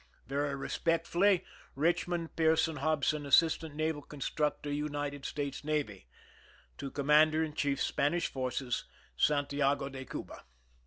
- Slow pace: Yes, slow, 110 wpm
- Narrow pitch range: Yes, narrow, 2.2 semitones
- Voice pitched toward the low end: No, medium, 150 Hz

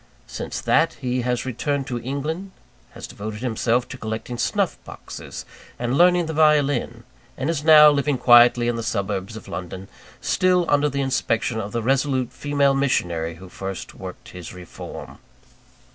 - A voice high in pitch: No, low, 125 Hz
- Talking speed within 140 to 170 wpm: Yes, average, 160 wpm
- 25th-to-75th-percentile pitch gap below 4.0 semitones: No, average, 4.5 semitones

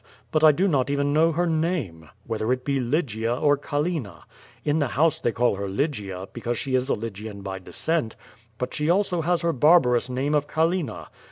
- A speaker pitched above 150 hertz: No, medium, 140 Hz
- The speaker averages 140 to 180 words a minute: No, average, 195 wpm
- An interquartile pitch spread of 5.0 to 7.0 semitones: Yes, wide, 5.6 semitones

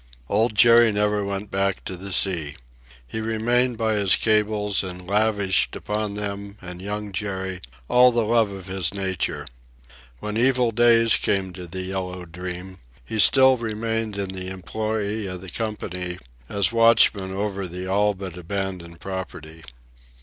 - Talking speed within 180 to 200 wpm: No, average, 150 wpm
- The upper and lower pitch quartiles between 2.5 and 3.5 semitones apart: Yes, average, 2.8 semitones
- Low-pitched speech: Yes, low, 100 Hz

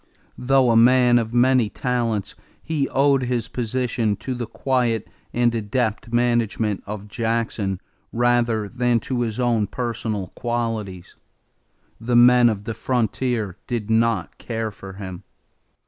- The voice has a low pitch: Yes, low, 115 Hz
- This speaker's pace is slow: Yes, slow, 130 wpm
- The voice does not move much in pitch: Yes, narrow, 2.3 semitones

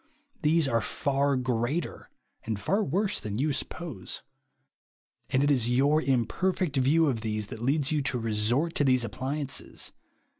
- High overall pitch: No, low, 135 Hz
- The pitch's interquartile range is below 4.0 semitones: No, average, 4.4 semitones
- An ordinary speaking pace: Yes, average, 155 wpm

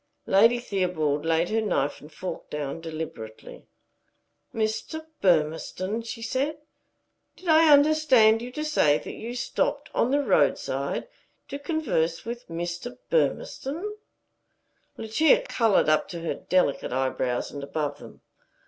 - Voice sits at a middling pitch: No, high, 215 Hz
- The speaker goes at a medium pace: No, slow, 130 wpm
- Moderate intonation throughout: No, wide, 8.9 semitones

